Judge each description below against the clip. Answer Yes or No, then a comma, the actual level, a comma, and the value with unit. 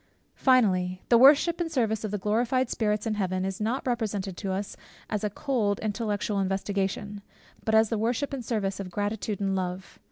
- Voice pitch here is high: Yes, high, 210 Hz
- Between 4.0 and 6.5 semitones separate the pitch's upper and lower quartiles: No, average, 3.1 semitones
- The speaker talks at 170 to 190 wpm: Yes, average, 180 wpm